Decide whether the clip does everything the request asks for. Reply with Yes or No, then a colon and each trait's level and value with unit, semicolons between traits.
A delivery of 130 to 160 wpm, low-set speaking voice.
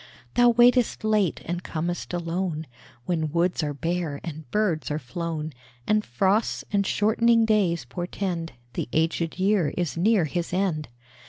No: average, 145 wpm; medium, 175 Hz